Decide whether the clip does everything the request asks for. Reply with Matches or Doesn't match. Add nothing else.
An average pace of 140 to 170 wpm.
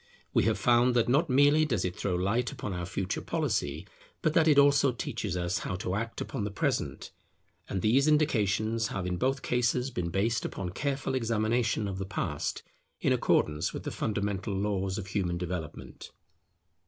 Doesn't match